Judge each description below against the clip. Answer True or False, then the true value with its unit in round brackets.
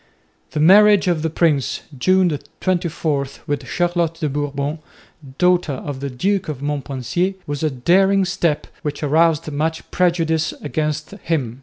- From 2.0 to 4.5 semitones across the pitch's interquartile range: True (3.3 semitones)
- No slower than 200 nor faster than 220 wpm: False (140 wpm)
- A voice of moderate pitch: True (160 Hz)